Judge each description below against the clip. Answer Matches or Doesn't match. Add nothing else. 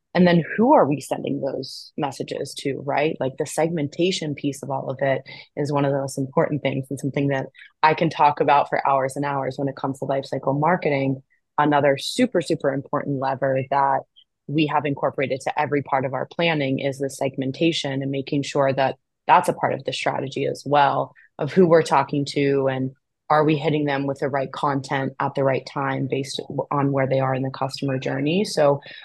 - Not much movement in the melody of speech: Matches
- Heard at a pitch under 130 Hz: Doesn't match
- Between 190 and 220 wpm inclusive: Matches